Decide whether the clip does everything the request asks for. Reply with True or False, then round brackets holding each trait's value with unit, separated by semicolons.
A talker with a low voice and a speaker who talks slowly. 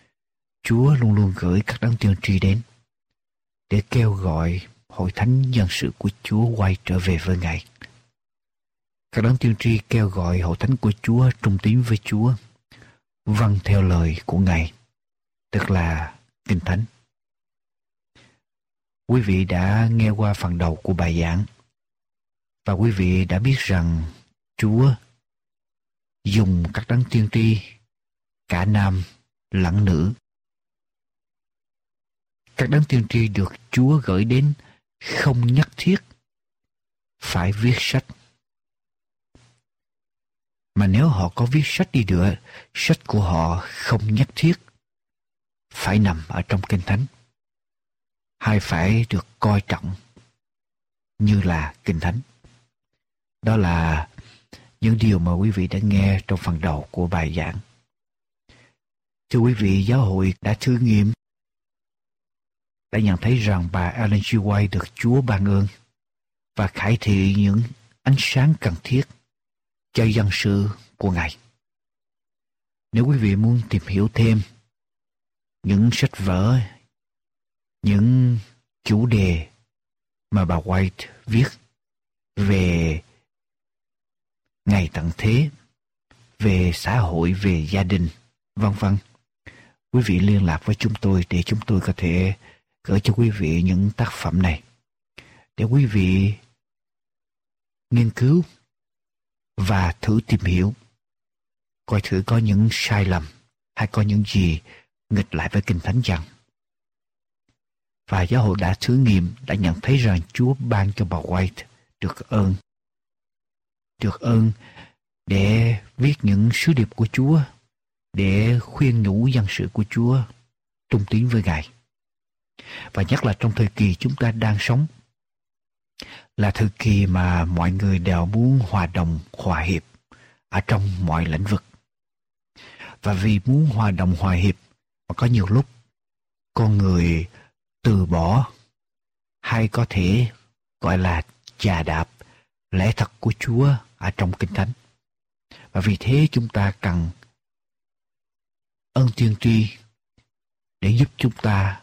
True (105 Hz; 135 wpm)